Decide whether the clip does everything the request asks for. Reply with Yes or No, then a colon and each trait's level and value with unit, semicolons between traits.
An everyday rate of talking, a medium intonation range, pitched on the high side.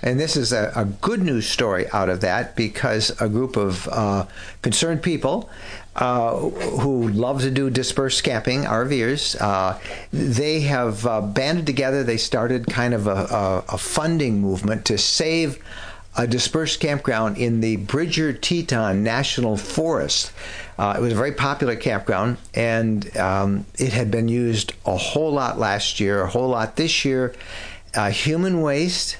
No: average, 160 wpm; average, 5.0 semitones; low, 120 Hz